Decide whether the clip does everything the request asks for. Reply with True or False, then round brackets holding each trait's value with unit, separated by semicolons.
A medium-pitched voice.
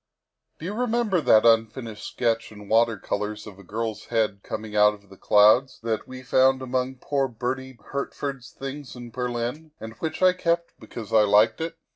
False (120 Hz)